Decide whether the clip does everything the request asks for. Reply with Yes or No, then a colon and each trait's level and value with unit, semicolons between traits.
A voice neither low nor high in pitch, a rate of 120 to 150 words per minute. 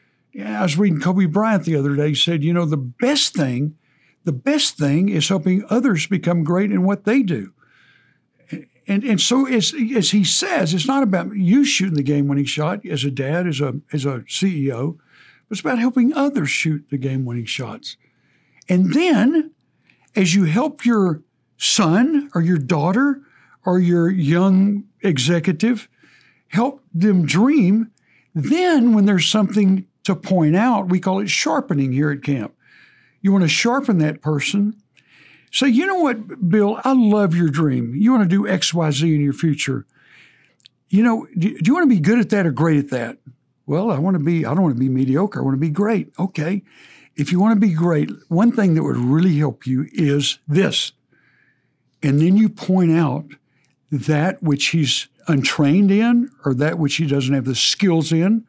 No: medium, 180 Hz; average, 185 wpm